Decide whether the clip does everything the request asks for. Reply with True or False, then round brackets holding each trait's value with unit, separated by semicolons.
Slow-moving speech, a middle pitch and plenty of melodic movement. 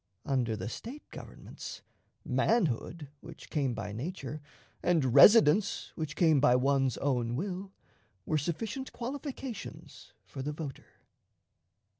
True (115 wpm; 150 Hz; 6.6 semitones)